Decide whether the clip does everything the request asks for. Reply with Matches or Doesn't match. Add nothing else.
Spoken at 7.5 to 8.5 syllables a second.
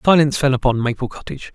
Matches